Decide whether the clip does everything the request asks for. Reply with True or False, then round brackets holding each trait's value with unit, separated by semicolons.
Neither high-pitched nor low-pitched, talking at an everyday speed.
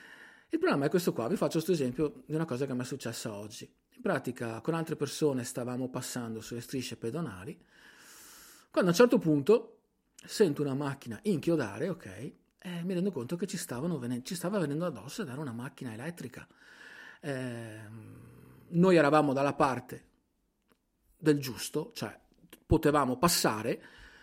True (145 Hz; 155 wpm)